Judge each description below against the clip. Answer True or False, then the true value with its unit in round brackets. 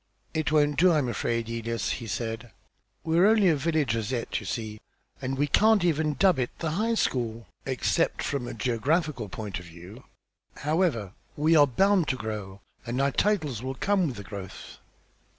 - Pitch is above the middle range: False (130 Hz)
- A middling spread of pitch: False (5.9 semitones)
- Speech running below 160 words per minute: False (180 wpm)